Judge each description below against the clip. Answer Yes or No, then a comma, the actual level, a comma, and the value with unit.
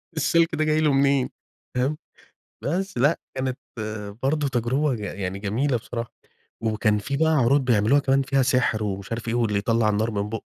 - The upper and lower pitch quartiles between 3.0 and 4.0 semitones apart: No, average, 4.4 semitones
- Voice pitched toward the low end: Yes, low, 125 Hz